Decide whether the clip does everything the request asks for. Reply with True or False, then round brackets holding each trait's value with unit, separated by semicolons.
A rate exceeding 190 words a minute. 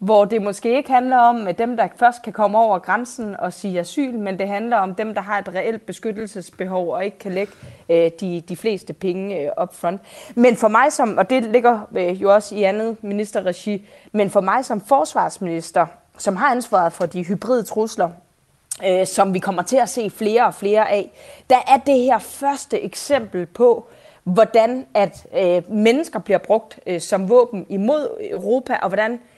False (180 wpm)